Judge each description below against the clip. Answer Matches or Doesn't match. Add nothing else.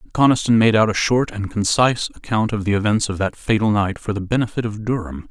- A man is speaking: Matches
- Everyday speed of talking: Doesn't match